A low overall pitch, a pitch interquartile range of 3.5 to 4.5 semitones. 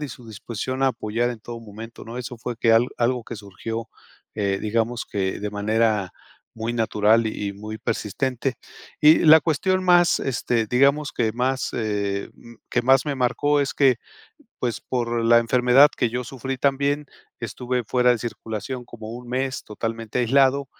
No: low, 120 Hz; average, 3.0 semitones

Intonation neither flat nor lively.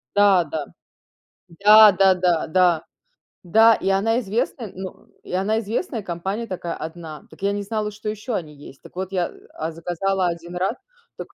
Yes: average, 3.6 semitones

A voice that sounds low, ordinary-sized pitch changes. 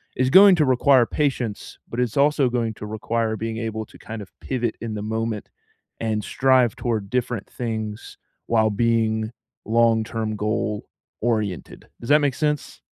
No: low, 115 Hz; narrow, 2.3 semitones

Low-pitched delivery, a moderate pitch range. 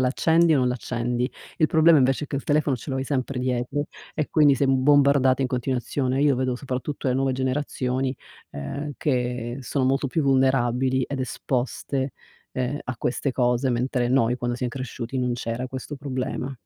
No: low, 130 Hz; narrow, 1.9 semitones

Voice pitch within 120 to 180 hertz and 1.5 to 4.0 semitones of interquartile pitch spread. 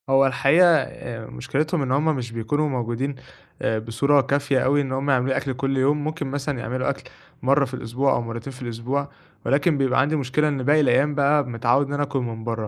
Yes: low, 135 Hz; average, 2.7 semitones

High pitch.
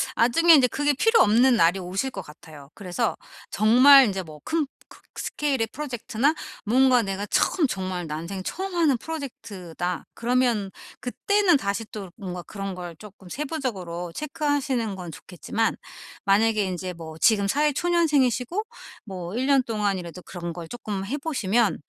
Yes: high, 220 Hz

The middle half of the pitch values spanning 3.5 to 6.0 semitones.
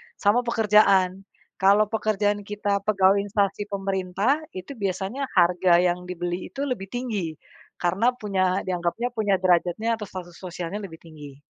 No: average, 2.7 semitones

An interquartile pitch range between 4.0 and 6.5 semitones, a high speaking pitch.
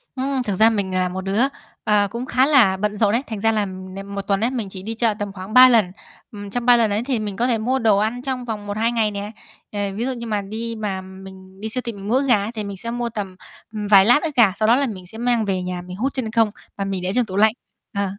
No: average, 3.1 semitones; high, 215 Hz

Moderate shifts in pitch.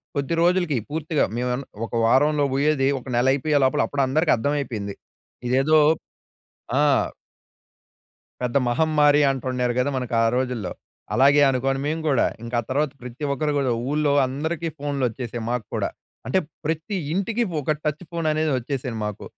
Yes: average, 3.4 semitones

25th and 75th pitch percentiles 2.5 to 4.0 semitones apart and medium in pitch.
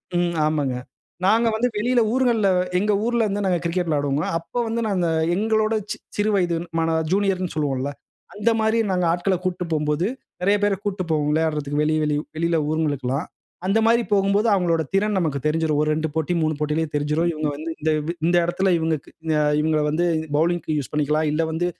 No: average, 4.5 semitones; medium, 170 Hz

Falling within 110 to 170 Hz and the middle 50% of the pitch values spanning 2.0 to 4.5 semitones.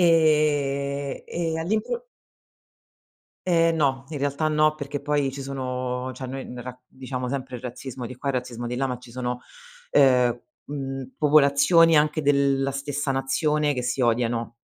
Yes: low, 135 Hz; average, 2.8 semitones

